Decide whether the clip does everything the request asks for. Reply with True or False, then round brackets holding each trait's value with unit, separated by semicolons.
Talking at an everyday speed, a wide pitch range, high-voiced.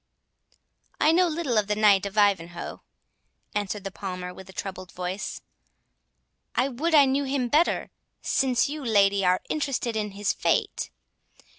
True (150 wpm; 6.0 semitones; 210 Hz)